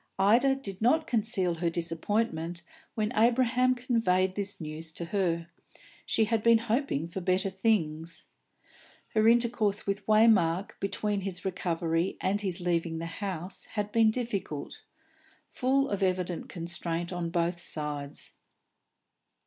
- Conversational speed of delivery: No, slow, 130 wpm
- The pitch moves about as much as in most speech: Yes, average, 4.6 semitones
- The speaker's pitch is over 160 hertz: Yes, high, 190 Hz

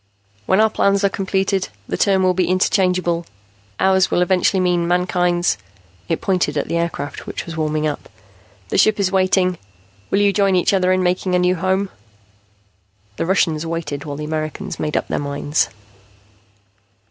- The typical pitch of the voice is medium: Yes, medium, 180 Hz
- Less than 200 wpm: Yes, average, 170 wpm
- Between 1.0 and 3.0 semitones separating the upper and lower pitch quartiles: Yes, narrow, 2.4 semitones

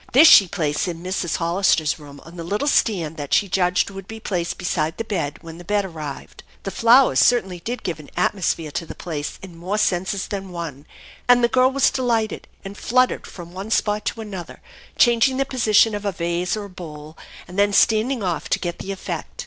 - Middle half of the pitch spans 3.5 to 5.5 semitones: Yes, average, 4.4 semitones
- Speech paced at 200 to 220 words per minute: Yes, fast, 205 wpm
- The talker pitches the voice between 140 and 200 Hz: Yes, high, 190 Hz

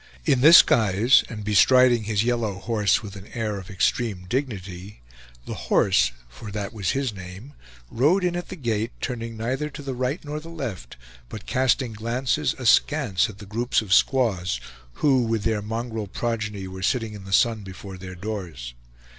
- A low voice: Yes, low, 110 Hz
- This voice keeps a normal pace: Yes, average, 175 wpm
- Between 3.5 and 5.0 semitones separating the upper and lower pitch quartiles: Yes, average, 4.4 semitones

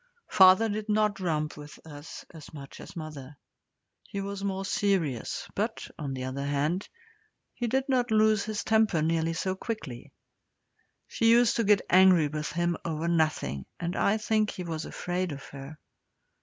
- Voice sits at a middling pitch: Yes, medium, 175 Hz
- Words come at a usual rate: Yes, average, 165 wpm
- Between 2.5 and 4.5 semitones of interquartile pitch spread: No, wide, 5.5 semitones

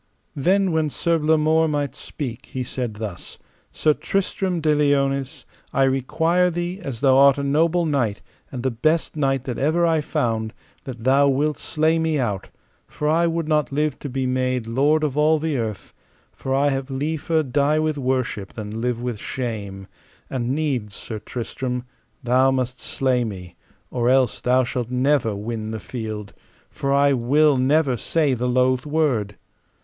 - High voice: No, low, 135 Hz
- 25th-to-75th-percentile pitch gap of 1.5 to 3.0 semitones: No, average, 3.9 semitones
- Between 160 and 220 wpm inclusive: Yes, average, 170 wpm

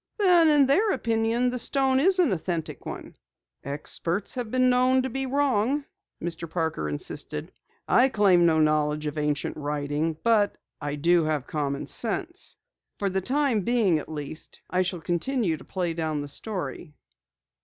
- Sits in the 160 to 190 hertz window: Yes, medium, 185 Hz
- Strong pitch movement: Yes, wide, 8.7 semitones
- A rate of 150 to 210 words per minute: Yes, average, 160 wpm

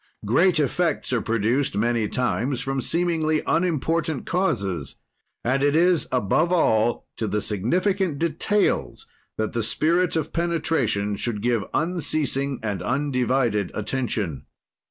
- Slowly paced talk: Yes, slow, 120 wpm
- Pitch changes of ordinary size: No, wide, 6.7 semitones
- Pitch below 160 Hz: Yes, low, 135 Hz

